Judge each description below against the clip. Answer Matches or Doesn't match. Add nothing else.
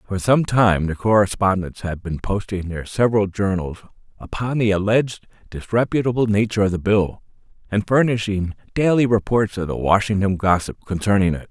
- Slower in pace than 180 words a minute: Matches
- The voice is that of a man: Matches